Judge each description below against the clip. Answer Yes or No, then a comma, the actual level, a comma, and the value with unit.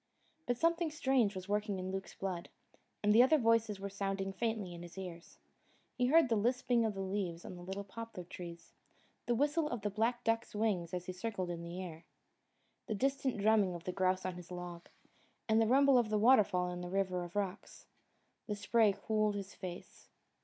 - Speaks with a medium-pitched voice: No, high, 200 Hz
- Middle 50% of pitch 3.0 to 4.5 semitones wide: Yes, average, 3.9 semitones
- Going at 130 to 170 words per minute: No, average, 195 wpm